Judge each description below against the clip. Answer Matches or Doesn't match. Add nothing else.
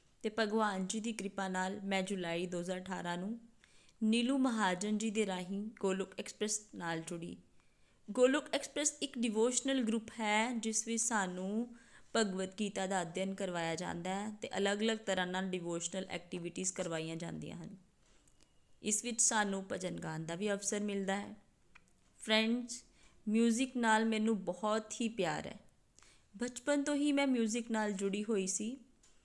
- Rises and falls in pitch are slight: Doesn't match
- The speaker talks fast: Doesn't match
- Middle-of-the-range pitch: Doesn't match